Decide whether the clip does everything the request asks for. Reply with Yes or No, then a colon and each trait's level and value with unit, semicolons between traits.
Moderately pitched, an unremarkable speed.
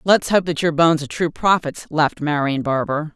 No: medium, 155 Hz; fast, 210 wpm